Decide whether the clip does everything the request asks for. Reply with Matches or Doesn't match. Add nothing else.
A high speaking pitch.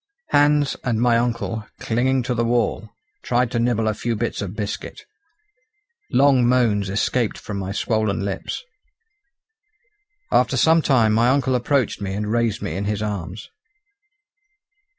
Doesn't match